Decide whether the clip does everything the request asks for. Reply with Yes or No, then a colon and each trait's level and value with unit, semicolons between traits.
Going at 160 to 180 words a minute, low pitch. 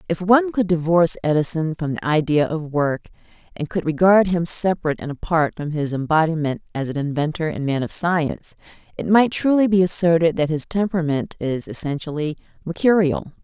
No: average, 170 wpm; medium, 165 Hz